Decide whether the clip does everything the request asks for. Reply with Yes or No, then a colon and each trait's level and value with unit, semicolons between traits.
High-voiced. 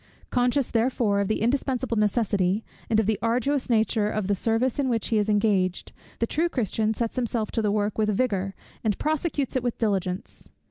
Yes: high, 220 Hz